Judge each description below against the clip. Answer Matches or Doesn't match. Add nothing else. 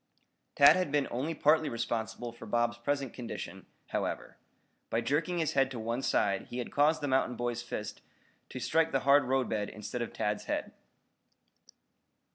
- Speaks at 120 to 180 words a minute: Matches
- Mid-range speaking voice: Doesn't match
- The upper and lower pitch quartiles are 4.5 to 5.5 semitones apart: Doesn't match